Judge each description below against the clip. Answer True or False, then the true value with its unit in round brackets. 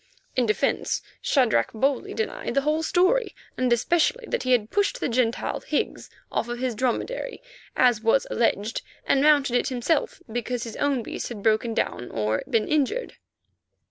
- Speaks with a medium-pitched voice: False (250 Hz)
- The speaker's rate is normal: True (160 wpm)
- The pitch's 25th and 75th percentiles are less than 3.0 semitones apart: False (4.9 semitones)